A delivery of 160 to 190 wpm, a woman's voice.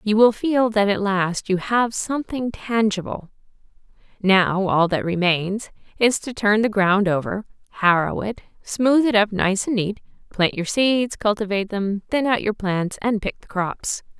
Yes: average, 175 wpm; female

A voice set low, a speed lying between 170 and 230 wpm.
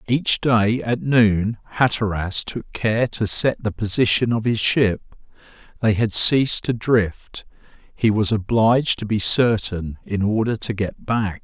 No: low, 110 Hz; average, 155 wpm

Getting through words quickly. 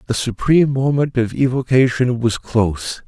No: slow, 135 wpm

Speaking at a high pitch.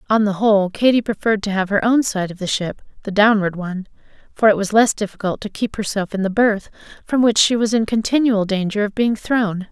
Yes: high, 210 Hz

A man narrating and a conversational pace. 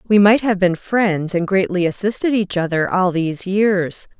No: female; average, 185 wpm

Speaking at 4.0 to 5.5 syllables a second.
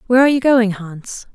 No: 6.1 syllables/s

